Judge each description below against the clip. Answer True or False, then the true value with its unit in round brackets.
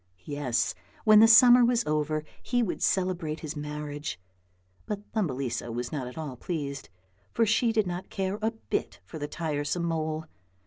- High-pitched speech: False (160 Hz)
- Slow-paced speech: False (165 wpm)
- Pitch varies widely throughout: True (6.2 semitones)